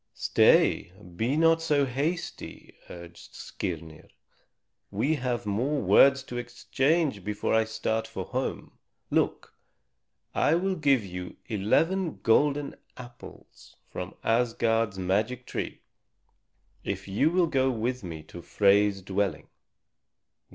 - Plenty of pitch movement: Yes, wide, 5.9 semitones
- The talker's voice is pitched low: Yes, low, 120 Hz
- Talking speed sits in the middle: No, slow, 115 wpm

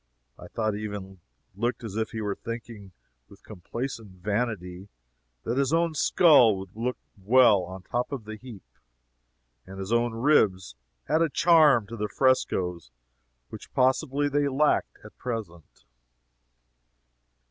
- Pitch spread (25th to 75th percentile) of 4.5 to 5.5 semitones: Yes, average, 4.8 semitones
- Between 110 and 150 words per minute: Yes, average, 140 wpm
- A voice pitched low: Yes, low, 115 Hz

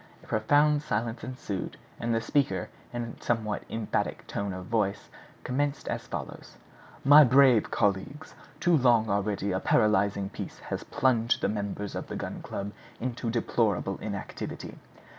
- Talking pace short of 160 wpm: Yes, average, 145 wpm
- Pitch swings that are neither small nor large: Yes, average, 4.0 semitones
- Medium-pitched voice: No, low, 115 Hz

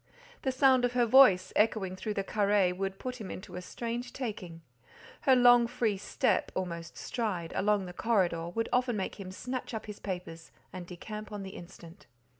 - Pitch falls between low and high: No, high, 205 Hz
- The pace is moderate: Yes, average, 175 wpm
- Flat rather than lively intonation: No, average, 4.5 semitones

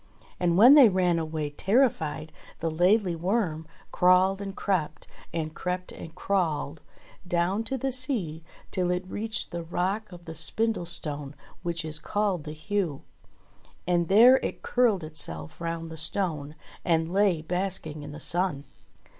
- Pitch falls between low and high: Yes, medium, 175 Hz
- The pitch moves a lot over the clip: No, average, 3.8 semitones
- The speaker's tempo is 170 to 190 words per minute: No, average, 145 wpm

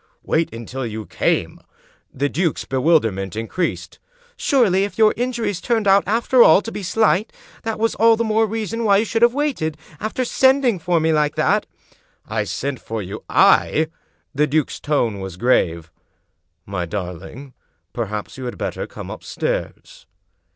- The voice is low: No, medium, 165 Hz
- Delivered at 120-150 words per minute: No, average, 180 wpm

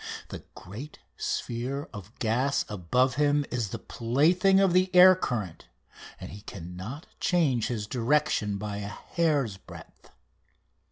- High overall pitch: No, low, 125 Hz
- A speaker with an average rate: No, slow, 130 wpm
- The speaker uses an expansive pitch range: Yes, wide, 6.4 semitones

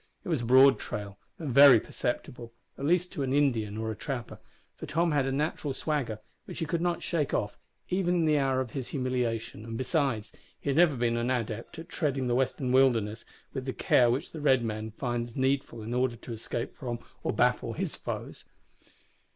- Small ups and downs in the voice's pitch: No, average, 3.5 semitones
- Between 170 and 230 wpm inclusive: Yes, fast, 205 wpm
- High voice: No, low, 130 Hz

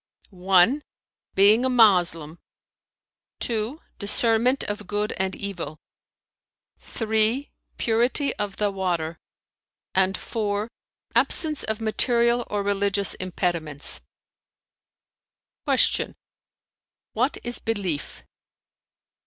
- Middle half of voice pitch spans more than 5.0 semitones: No, average, 3.8 semitones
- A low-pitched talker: No, high, 205 Hz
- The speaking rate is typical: No, slow, 85 wpm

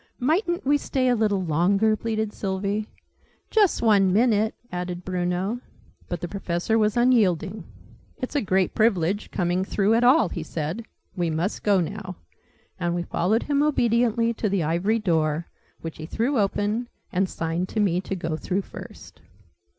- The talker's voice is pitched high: Yes, high, 200 Hz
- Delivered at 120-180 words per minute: Yes, average, 160 wpm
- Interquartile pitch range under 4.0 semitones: No, average, 4.4 semitones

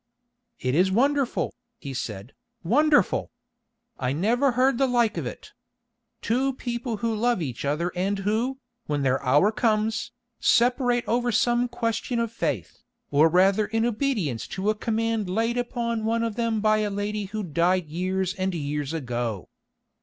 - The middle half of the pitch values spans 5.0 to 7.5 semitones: Yes, wide, 5.6 semitones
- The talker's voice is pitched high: Yes, high, 215 Hz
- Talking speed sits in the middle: Yes, average, 155 wpm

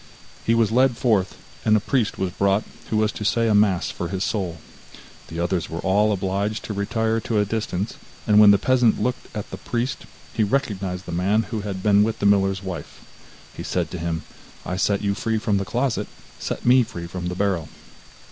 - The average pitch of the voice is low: Yes, low, 100 Hz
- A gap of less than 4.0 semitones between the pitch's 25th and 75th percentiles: Yes, average, 3.0 semitones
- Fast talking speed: Yes, fast, 210 wpm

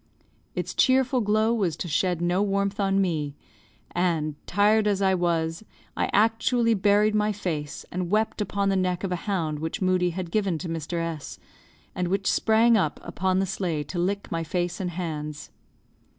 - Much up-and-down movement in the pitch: No, average, 3.4 semitones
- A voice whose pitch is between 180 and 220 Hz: Yes, medium, 185 Hz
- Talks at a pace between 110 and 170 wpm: No, average, 180 wpm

